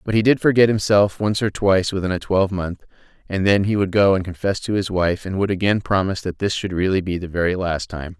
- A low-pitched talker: Yes, very low, 95 Hz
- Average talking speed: No, fast, 250 wpm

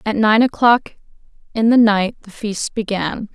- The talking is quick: No, average, 160 wpm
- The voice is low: No, high, 215 Hz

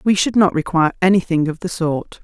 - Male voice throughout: No, female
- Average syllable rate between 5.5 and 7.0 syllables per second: Yes, 5.9 syllables/s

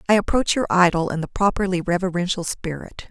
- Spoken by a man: No, female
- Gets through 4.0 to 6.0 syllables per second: Yes, 5.9 syllables/s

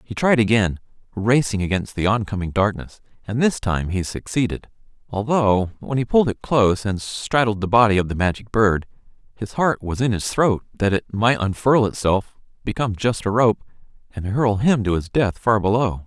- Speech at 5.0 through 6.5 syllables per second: Yes, 5.1 syllables/s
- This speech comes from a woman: No, male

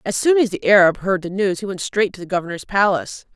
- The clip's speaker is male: No, female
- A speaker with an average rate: No, fast, 270 wpm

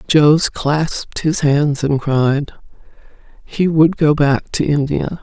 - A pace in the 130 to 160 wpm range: Yes, average, 140 wpm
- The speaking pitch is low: No, medium, 150 Hz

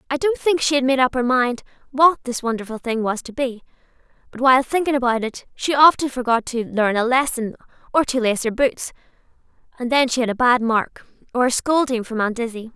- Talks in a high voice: Yes, very high, 250 Hz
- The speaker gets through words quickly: Yes, fast, 215 wpm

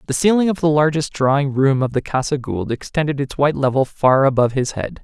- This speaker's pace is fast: Yes, fast, 225 wpm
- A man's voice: Yes, male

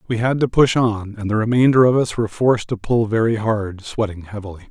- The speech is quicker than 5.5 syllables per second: Yes, 5.9 syllables/s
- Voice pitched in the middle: No, low, 110 Hz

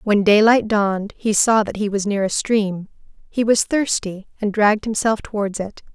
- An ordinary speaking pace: Yes, average, 190 wpm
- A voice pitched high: Yes, high, 210 Hz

